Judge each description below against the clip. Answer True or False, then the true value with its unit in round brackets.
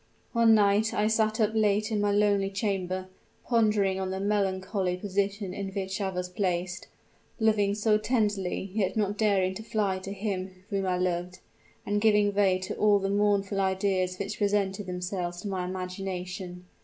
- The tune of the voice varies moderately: False (1.9 semitones)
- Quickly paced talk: False (170 wpm)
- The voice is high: True (195 Hz)